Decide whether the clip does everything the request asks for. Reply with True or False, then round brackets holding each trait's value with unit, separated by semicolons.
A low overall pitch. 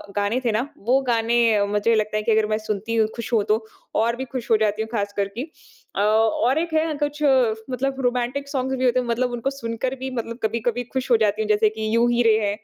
False (230 Hz)